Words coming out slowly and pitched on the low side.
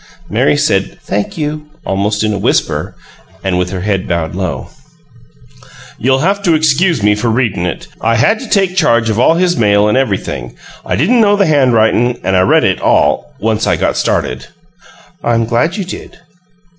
No: average, 180 wpm; low, 115 Hz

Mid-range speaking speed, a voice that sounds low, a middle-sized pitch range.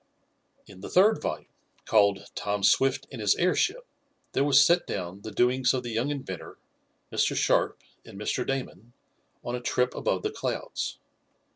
Yes: average, 160 wpm; low, 125 Hz; average, 4.9 semitones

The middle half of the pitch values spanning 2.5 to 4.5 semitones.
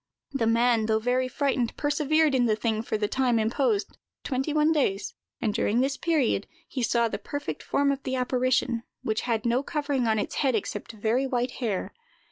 Yes: average, 3.4 semitones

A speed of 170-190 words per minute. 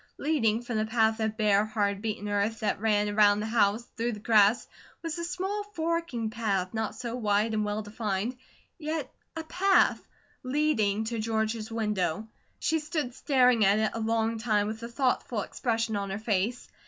Yes: average, 180 wpm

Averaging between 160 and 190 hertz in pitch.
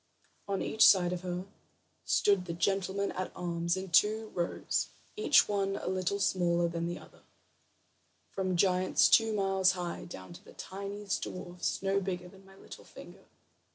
Yes: medium, 185 Hz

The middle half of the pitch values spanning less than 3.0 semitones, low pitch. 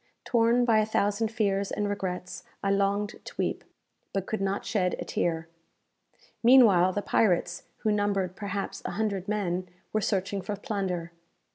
No: narrow, 2.4 semitones; high, 200 Hz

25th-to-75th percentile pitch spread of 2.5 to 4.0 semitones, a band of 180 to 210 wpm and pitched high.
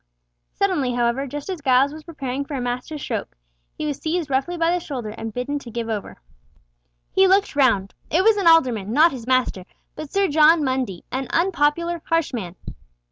No: average, 5.0 semitones; average, 190 wpm; very high, 280 Hz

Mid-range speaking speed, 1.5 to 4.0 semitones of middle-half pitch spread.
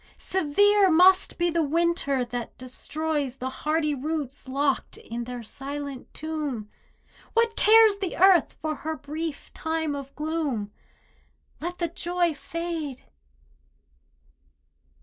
No: slow, 115 wpm; average, 3.7 semitones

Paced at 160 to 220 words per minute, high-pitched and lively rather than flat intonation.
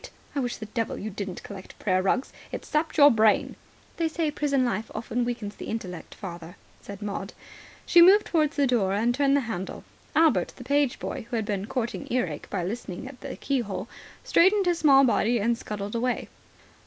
Yes: average, 190 wpm; high, 235 Hz; wide, 5.7 semitones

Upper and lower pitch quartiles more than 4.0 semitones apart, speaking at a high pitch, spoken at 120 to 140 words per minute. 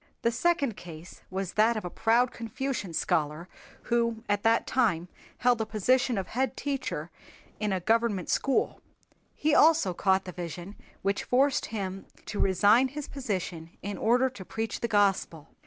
No: average, 4.7 semitones; high, 215 Hz; average, 160 wpm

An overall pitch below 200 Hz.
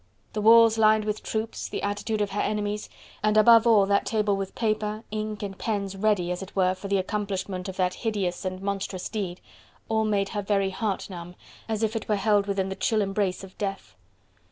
No: high, 205 Hz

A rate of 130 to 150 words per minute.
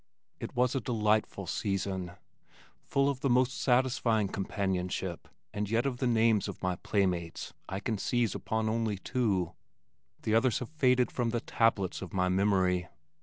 No: average, 160 wpm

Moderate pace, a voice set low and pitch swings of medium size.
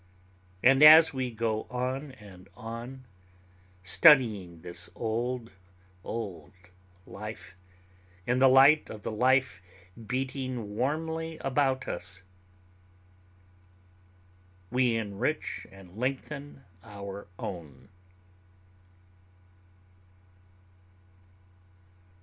No: slow, 75 wpm; low, 120 Hz; average, 4.7 semitones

